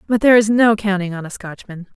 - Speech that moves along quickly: Yes, fast, 240 wpm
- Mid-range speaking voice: No, high, 200 Hz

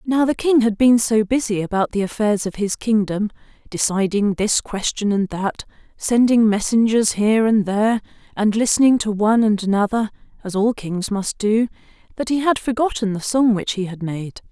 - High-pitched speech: Yes, high, 215 Hz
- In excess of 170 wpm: Yes, average, 180 wpm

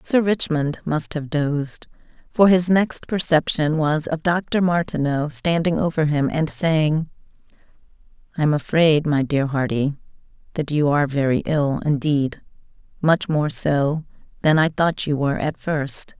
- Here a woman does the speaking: Yes, female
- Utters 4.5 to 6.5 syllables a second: No, 4.2 syllables/s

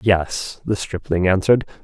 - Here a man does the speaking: Yes, male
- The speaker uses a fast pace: No, slow, 130 wpm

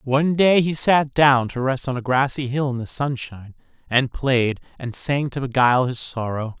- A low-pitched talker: Yes, low, 130 Hz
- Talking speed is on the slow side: No, average, 200 wpm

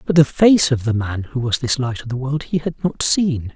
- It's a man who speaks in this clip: Yes, male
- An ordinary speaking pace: No, fast, 285 wpm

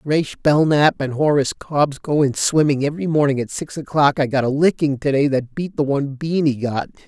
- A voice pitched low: No, medium, 145 Hz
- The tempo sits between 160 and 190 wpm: No, fast, 205 wpm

